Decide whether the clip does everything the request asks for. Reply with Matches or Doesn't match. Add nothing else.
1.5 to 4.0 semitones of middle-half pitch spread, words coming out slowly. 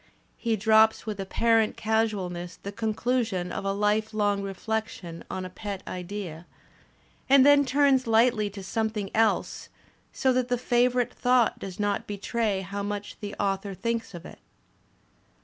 Doesn't match